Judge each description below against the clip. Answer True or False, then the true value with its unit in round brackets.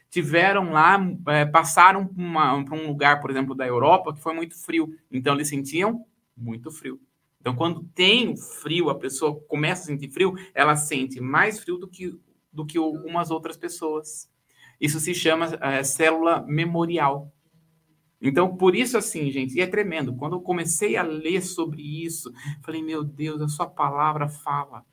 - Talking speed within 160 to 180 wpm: True (165 wpm)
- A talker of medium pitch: True (160 Hz)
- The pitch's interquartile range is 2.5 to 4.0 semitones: True (3.0 semitones)